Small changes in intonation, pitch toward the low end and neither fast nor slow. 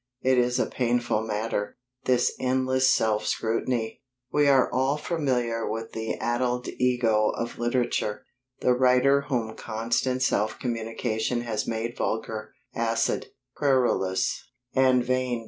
No: narrow, 2.3 semitones; low, 120 Hz; slow, 125 wpm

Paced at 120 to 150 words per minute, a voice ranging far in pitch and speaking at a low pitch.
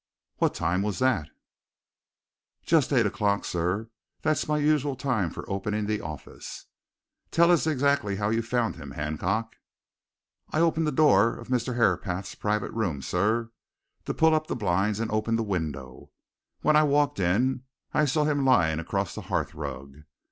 No: average, 160 wpm; wide, 6.8 semitones; low, 110 Hz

